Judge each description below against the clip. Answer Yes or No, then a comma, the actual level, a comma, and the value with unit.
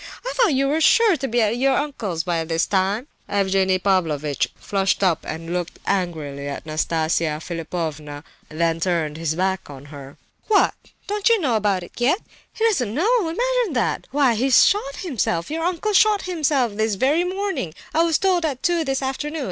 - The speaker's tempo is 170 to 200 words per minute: Yes, average, 180 wpm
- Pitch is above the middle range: Yes, high, 220 Hz